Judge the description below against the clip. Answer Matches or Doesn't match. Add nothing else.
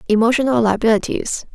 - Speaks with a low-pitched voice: Doesn't match